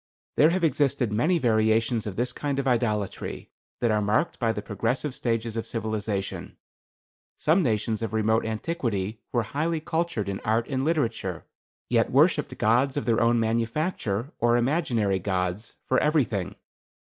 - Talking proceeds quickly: No, average, 150 wpm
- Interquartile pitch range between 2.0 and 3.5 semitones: No, average, 4.2 semitones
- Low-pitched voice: Yes, low, 115 Hz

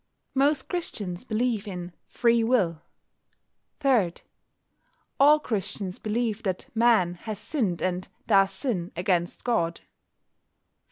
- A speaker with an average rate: No, slow, 105 wpm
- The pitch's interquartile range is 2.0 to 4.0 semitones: No, average, 4.9 semitones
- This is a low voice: No, high, 210 Hz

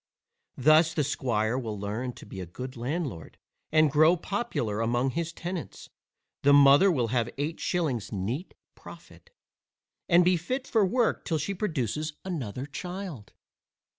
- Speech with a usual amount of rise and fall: No, wide, 6.4 semitones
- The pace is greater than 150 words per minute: No, average, 145 wpm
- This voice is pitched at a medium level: Yes, medium, 145 Hz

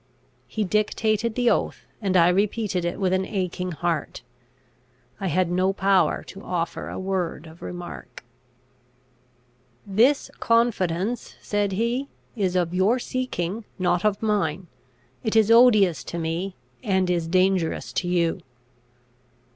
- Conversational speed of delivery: No, slow, 130 wpm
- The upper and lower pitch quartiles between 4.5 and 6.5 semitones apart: No, average, 3.3 semitones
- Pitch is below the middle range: No, high, 190 Hz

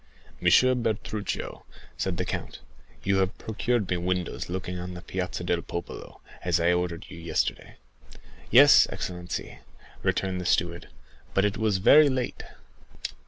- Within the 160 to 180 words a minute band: No, average, 140 wpm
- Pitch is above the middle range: No, very low, 90 Hz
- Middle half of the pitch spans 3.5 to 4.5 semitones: No, average, 2.9 semitones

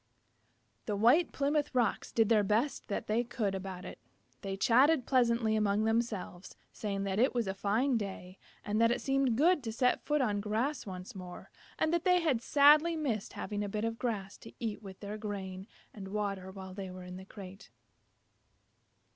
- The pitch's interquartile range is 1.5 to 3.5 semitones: No, average, 4.2 semitones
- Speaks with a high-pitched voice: Yes, high, 215 Hz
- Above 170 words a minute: Yes, average, 190 wpm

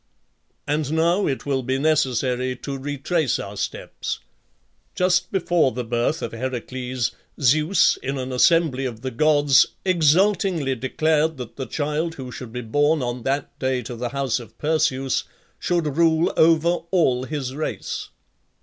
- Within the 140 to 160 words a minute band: Yes, average, 150 wpm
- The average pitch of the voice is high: No, medium, 140 Hz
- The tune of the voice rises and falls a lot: No, average, 3.8 semitones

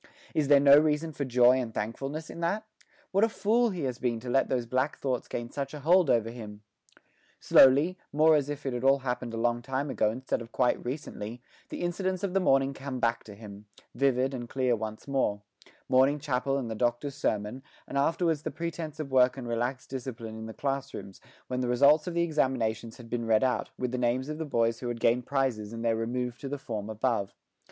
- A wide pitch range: No, average, 3.4 semitones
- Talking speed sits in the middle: No, fast, 225 wpm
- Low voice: Yes, low, 130 Hz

